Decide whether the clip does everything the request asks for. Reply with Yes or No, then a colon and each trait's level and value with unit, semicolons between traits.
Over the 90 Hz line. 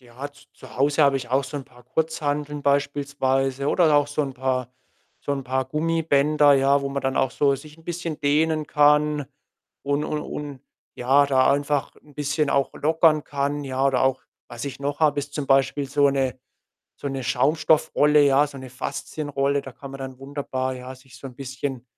Yes: medium, 140 Hz